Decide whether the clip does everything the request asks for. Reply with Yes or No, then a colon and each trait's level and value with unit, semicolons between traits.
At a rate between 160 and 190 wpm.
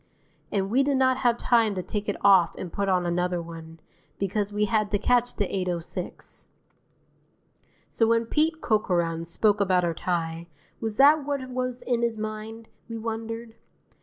Yes: average, 165 wpm